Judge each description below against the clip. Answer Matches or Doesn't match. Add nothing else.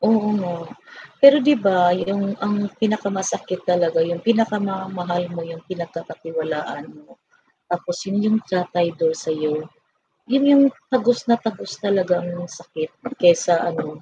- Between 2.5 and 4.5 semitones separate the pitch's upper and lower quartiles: Matches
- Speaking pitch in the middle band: Matches